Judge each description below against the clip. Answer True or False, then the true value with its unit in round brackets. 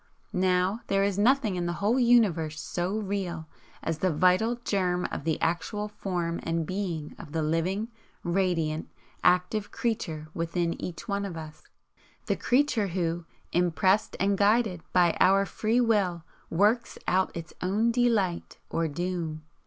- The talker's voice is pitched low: False (185 Hz)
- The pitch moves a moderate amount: True (3.6 semitones)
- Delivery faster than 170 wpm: False (145 wpm)